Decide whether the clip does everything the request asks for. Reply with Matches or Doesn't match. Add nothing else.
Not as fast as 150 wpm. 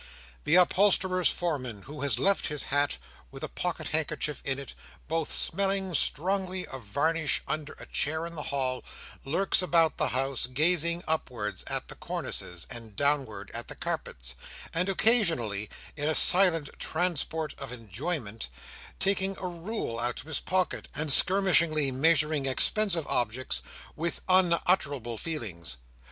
Matches